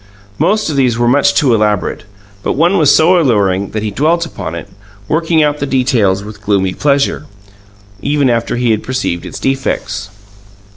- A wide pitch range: Yes, wide, 6.1 semitones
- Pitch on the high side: No, low, 125 Hz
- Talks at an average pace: Yes, average, 175 wpm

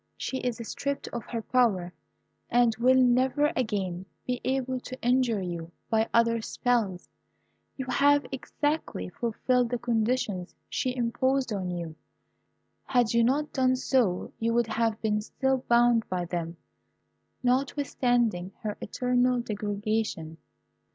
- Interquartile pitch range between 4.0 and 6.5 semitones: No, average, 3.4 semitones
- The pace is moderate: No, slow, 130 wpm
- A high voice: Yes, high, 235 Hz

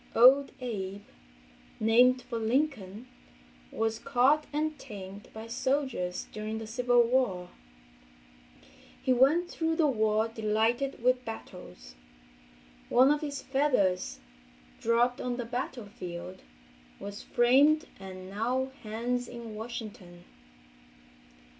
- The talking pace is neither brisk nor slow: No, slow, 100 wpm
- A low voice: No, high, 230 Hz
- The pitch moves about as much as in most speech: Yes, average, 4.2 semitones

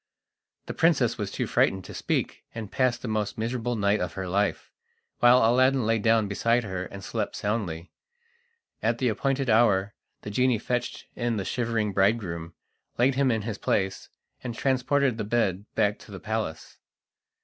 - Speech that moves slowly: No, average, 170 wpm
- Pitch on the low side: Yes, low, 110 Hz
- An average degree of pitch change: Yes, average, 3.3 semitones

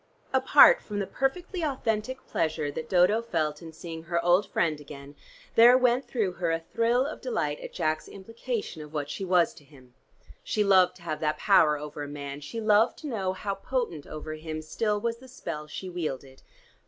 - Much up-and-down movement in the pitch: Yes, wide, 6.9 semitones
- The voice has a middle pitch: Yes, medium, 180 Hz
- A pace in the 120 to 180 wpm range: No, average, 195 wpm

